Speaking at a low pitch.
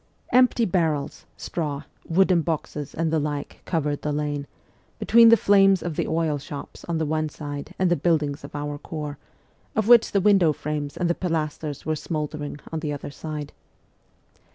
No: medium, 155 Hz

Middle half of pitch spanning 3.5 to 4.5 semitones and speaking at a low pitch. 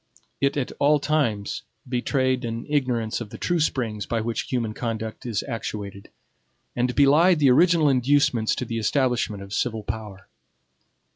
Yes: average, 4.2 semitones; low, 120 Hz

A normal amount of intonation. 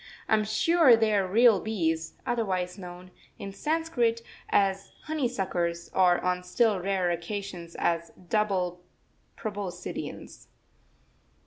Yes: average, 3.8 semitones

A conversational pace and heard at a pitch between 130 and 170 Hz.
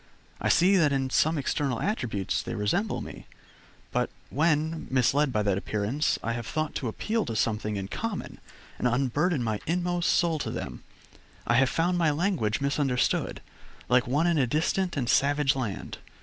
Yes: average, 170 wpm; medium, 140 Hz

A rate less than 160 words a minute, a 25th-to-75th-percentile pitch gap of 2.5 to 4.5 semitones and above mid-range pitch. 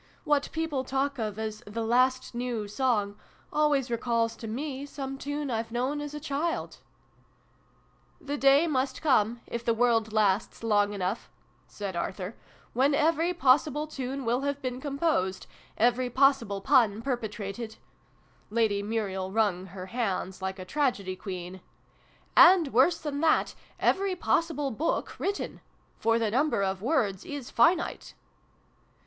No: average, 150 wpm; average, 5.1 semitones; high, 245 Hz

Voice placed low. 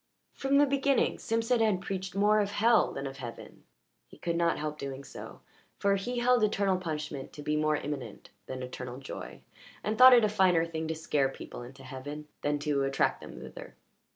No: medium, 165 Hz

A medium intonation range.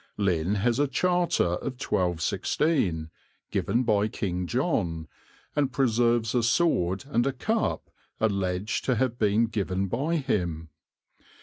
No: wide, 6.2 semitones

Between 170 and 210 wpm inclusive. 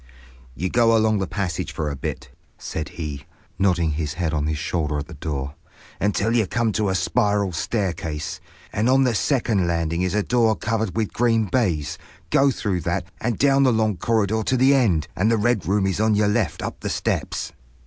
Yes: average, 200 wpm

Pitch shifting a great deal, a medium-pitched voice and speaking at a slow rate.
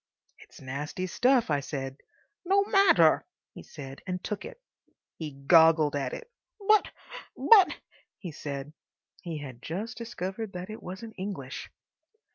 Yes: wide, 7.9 semitones; medium, 180 Hz; slow, 130 wpm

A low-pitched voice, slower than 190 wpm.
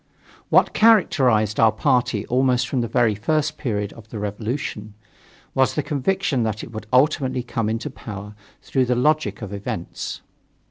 Yes: low, 120 Hz; average, 155 wpm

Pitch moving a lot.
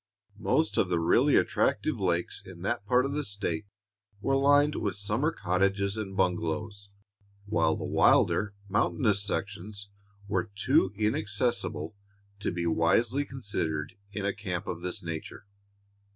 No: average, 3.3 semitones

